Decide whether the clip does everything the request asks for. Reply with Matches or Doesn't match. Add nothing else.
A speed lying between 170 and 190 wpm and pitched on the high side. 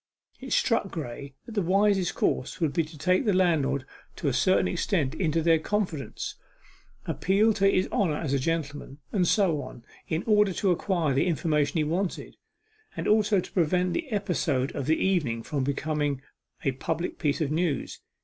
Doesn't match